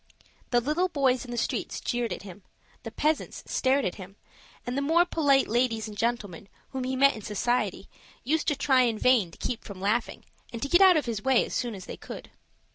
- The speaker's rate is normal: No, fast, 220 wpm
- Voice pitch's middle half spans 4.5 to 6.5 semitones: No, average, 4.1 semitones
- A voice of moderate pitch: No, high, 245 Hz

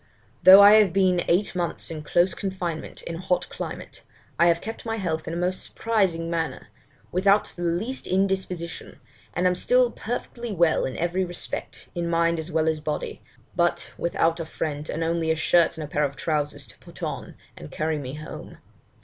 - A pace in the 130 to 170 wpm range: No, average, 190 wpm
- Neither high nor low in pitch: Yes, medium, 170 Hz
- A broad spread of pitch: No, average, 2.8 semitones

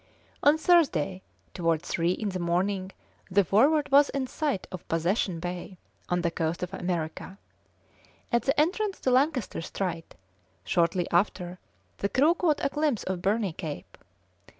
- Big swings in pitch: Yes, wide, 7.9 semitones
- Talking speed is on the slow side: No, average, 150 wpm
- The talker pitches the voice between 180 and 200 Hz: Yes, high, 190 Hz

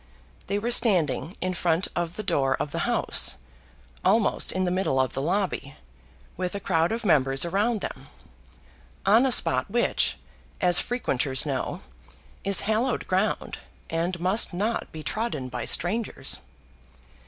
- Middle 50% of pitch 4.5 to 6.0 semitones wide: Yes, average, 5.3 semitones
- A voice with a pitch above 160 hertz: Yes, medium, 185 Hz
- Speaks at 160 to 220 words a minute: No, average, 145 wpm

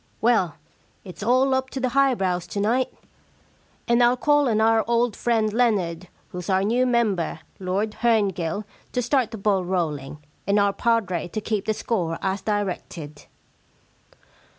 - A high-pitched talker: Yes, high, 210 Hz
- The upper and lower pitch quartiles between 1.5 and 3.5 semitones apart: No, average, 4.4 semitones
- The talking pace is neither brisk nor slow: Yes, average, 155 wpm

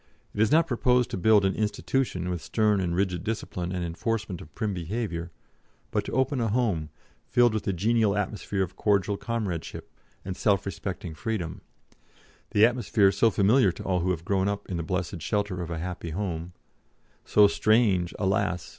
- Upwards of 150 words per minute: Yes, average, 180 wpm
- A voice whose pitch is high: No, low, 100 Hz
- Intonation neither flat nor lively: Yes, average, 3.7 semitones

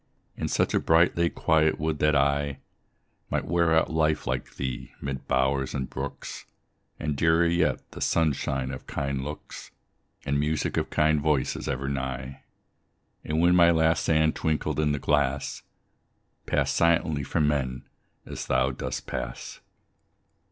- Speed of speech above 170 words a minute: No, average, 150 wpm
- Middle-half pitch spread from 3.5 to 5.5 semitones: No, average, 2.9 semitones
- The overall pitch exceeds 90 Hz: No, very low, 75 Hz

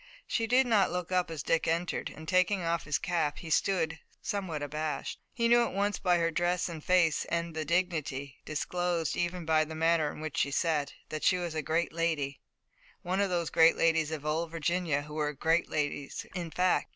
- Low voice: No, medium, 165 Hz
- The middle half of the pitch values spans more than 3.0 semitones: No, narrow, 2.5 semitones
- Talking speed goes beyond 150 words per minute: Yes, fast, 205 wpm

